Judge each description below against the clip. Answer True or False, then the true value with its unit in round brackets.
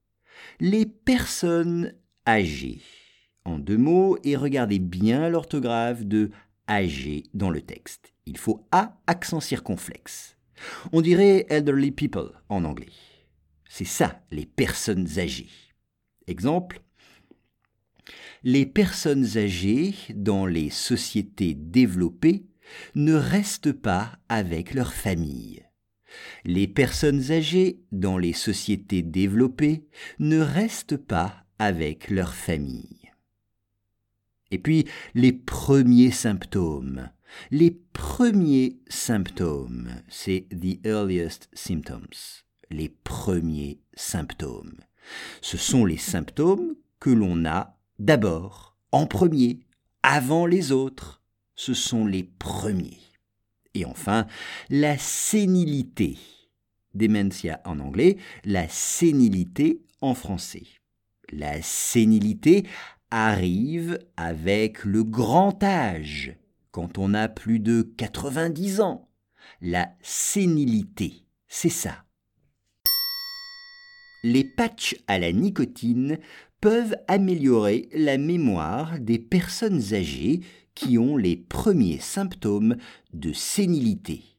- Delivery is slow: True (100 wpm)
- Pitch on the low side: True (115 Hz)